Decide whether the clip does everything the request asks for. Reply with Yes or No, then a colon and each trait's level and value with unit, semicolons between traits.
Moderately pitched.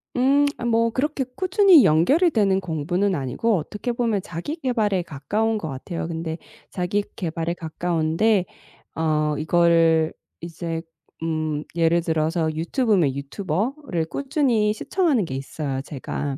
Yes: medium, 175 Hz